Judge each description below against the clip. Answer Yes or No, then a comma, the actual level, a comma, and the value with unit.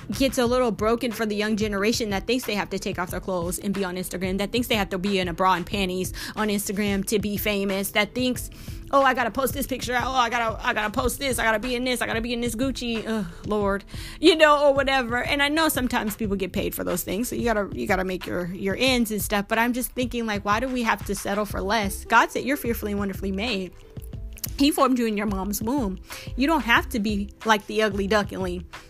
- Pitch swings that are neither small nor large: Yes, average, 3.7 semitones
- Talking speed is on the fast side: Yes, fast, 260 wpm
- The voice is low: No, high, 220 Hz